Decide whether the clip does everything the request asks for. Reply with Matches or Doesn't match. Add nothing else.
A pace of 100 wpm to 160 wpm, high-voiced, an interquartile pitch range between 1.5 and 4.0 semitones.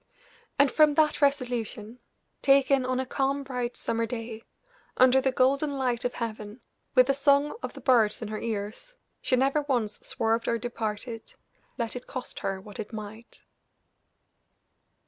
Matches